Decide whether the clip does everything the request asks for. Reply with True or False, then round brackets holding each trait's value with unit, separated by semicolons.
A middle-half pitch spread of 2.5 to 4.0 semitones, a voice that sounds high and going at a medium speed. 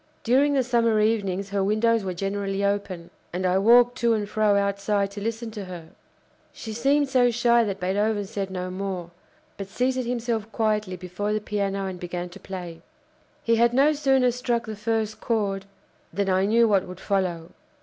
True (3.2 semitones; 205 Hz; 180 wpm)